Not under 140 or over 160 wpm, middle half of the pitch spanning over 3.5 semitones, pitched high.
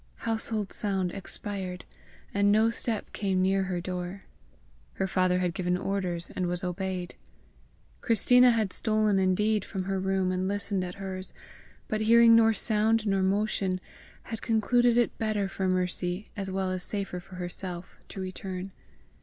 No: average, 155 wpm; narrow, 2.6 semitones; high, 195 Hz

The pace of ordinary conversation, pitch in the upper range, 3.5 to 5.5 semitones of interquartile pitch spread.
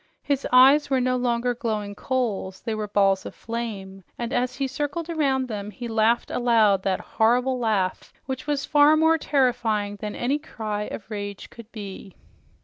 Yes: average, 170 wpm; high, 235 Hz; average, 4.1 semitones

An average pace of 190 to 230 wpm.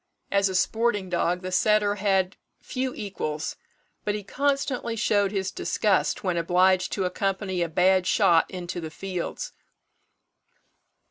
No: slow, 135 wpm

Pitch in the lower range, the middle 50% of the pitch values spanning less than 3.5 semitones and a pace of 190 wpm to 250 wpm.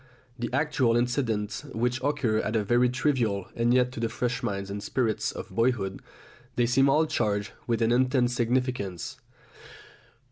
No: low, 120 Hz; narrow, 2.6 semitones; average, 150 wpm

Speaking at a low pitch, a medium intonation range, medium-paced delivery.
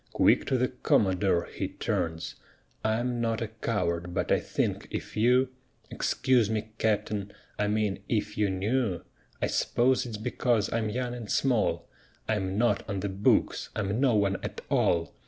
Yes: low, 110 Hz; average, 3.4 semitones; average, 160 wpm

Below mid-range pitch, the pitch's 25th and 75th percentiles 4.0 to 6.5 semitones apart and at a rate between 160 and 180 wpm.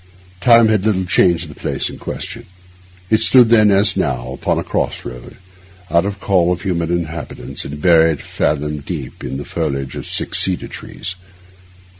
Yes: very low, 85 Hz; average, 5.0 semitones; average, 170 wpm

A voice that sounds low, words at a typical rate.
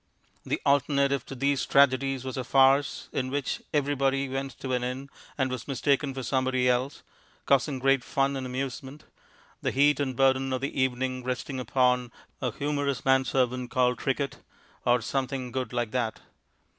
Yes: low, 130 Hz; average, 165 wpm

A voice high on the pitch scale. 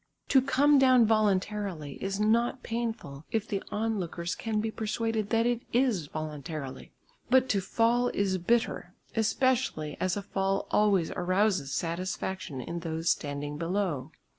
Yes: high, 200 Hz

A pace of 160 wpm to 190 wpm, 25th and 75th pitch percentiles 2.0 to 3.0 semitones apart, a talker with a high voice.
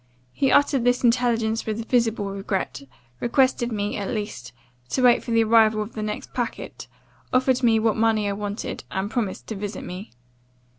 Yes: average, 170 wpm; average, 2.7 semitones; high, 220 Hz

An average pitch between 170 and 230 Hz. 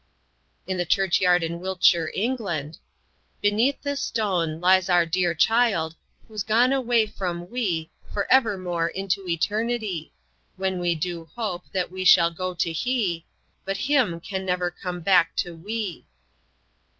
Yes: medium, 185 Hz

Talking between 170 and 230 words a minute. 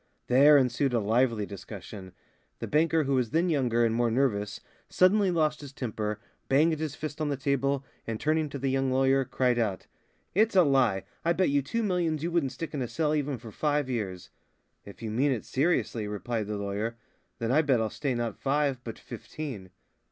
Yes: average, 200 wpm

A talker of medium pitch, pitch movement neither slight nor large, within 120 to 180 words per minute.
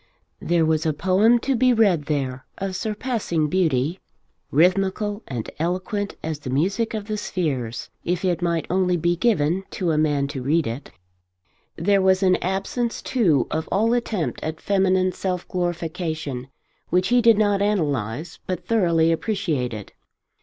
Yes: medium, 180 Hz; average, 4.4 semitones; average, 155 wpm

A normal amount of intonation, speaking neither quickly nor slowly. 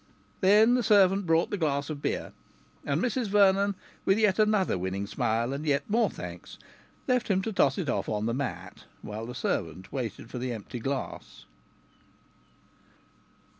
No: wide, 8.9 semitones; average, 165 wpm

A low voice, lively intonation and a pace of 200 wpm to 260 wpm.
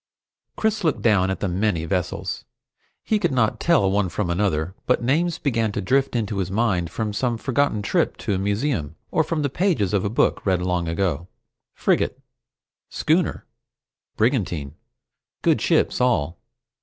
No: low, 105 Hz; wide, 6.3 semitones; average, 160 wpm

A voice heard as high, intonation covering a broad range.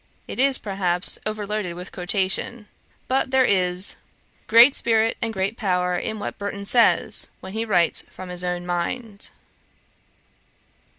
No: high, 200 Hz; average, 3.9 semitones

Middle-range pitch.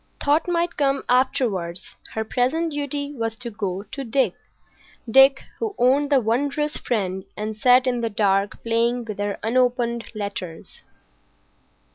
No: high, 245 Hz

